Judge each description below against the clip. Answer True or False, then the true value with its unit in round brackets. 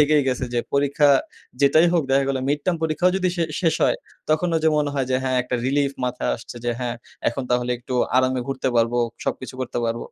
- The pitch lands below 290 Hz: True (135 Hz)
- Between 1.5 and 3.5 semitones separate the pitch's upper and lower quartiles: True (3.2 semitones)